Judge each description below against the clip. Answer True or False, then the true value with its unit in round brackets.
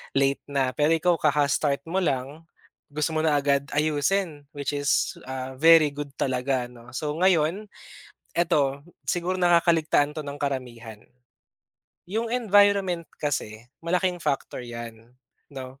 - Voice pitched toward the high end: False (145 Hz)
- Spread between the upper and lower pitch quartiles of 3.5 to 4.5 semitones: True (3.9 semitones)